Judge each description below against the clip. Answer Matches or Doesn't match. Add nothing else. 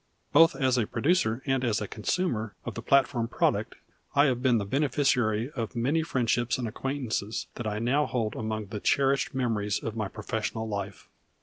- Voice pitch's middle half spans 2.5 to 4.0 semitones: Matches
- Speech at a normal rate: Matches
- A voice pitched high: Doesn't match